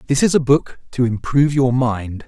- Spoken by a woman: No, male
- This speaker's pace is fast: Yes, fast, 210 wpm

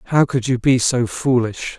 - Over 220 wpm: No, average, 200 wpm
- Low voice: Yes, low, 125 Hz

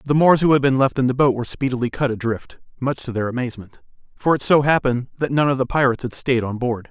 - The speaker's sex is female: No, male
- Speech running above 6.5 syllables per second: Yes, 6.7 syllables/s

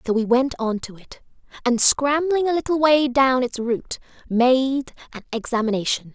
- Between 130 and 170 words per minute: Yes, average, 165 wpm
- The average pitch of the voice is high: Yes, very high, 255 Hz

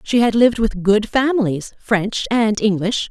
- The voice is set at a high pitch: Yes, high, 220 Hz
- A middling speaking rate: Yes, average, 175 wpm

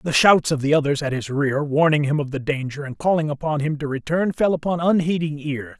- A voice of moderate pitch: Yes, medium, 150 Hz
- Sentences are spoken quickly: Yes, fast, 240 wpm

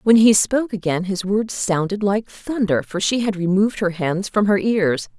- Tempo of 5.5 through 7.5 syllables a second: No, 4.8 syllables/s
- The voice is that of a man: No, female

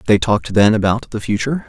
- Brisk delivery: Yes, fast, 215 wpm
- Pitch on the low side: Yes, low, 110 Hz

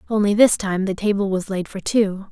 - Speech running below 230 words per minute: No, fast, 235 wpm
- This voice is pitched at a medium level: No, high, 200 Hz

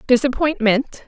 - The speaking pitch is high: Yes, very high, 250 Hz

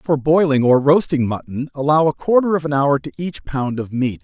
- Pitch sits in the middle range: Yes, medium, 145 Hz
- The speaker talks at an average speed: No, fast, 225 wpm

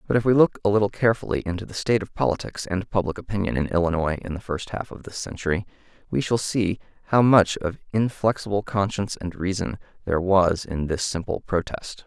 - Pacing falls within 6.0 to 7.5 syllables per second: Yes, 6.1 syllables/s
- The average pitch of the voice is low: Yes, very low, 95 Hz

